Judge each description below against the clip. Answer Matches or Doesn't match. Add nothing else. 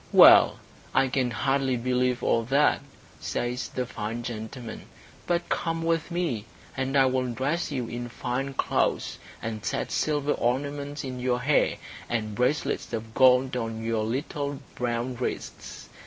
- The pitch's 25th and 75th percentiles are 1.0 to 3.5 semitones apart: Matches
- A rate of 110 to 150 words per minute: Matches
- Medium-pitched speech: Doesn't match